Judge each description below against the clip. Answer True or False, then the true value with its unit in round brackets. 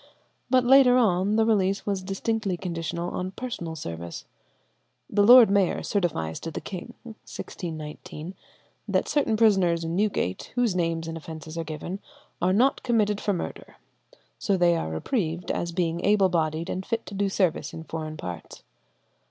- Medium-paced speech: True (160 wpm)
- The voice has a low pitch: False (185 Hz)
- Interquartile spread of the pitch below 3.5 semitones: False (4.2 semitones)